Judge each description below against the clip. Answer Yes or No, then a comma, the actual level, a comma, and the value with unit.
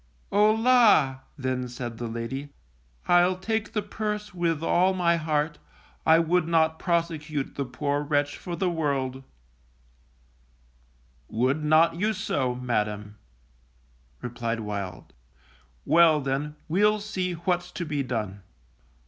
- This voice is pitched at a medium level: Yes, medium, 155 Hz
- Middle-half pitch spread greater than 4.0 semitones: Yes, wide, 5.5 semitones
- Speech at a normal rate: No, slow, 125 wpm